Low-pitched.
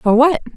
No: very high, 265 Hz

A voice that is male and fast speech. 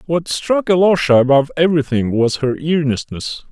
No: male; slow, 135 wpm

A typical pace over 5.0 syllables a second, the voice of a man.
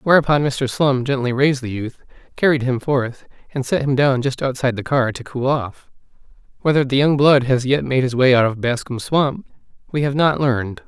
Yes: 5.3 syllables/s; male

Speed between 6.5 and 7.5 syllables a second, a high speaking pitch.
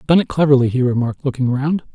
No: 7.0 syllables/s; low, 135 Hz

